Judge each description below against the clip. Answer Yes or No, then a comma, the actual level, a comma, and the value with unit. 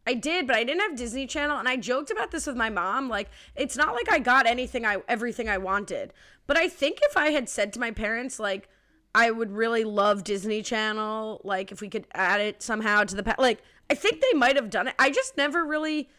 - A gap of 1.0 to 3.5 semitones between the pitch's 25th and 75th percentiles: No, average, 5.1 semitones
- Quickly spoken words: Yes, fast, 245 wpm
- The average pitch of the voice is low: No, high, 240 Hz